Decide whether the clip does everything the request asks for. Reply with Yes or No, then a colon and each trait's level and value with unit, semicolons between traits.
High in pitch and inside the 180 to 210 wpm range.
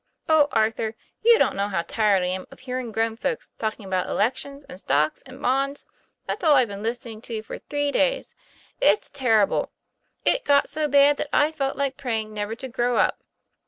Yes: high, 245 Hz; average, 195 wpm